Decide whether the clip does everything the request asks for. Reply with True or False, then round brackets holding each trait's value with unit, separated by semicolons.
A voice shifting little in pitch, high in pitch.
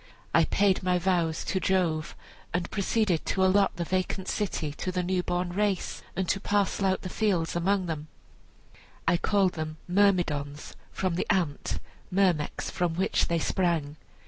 False (2.3 semitones; 180 Hz)